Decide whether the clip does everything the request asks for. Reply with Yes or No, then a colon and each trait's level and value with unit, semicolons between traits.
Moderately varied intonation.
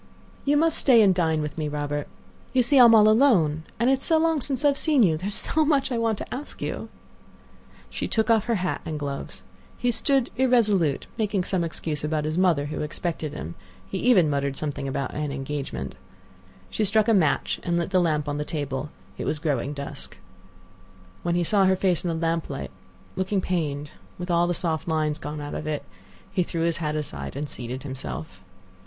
No: wide, 6.5 semitones